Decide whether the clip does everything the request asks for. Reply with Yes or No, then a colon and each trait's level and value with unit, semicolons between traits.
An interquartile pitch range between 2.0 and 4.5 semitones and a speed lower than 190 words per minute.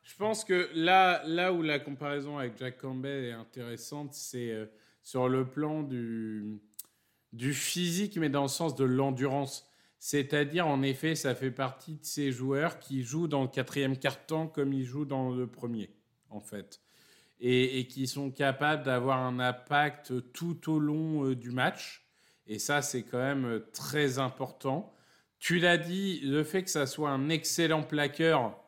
Yes: average, 3.3 semitones; average, 165 wpm